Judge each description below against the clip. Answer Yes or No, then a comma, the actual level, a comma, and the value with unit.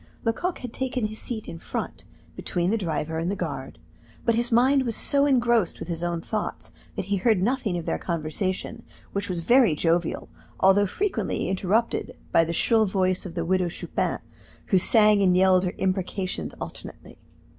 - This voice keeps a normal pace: Yes, average, 175 wpm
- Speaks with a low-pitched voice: No, high, 190 Hz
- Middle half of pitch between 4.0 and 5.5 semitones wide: Yes, average, 4.5 semitones